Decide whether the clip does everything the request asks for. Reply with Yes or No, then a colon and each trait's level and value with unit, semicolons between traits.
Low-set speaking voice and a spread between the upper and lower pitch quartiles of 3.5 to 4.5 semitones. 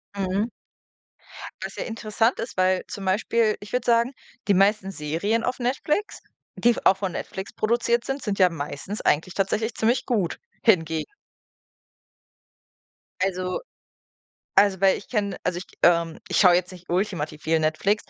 No: high, 195 Hz; average, 4.1 semitones